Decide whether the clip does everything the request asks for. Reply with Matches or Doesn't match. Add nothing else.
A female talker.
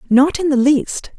Matches